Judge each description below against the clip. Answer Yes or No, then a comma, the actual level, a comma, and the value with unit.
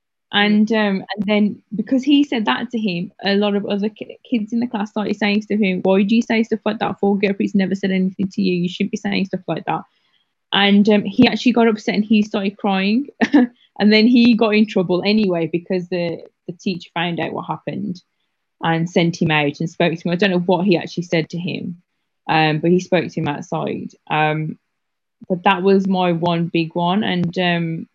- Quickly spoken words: Yes, fast, 220 wpm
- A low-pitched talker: No, high, 200 Hz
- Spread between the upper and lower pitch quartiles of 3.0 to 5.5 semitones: Yes, average, 3.3 semitones